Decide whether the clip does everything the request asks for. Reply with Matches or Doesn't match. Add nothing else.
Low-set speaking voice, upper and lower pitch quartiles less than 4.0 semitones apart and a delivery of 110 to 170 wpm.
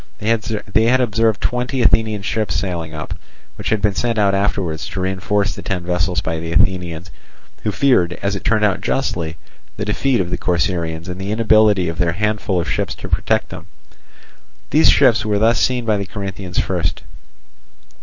Doesn't match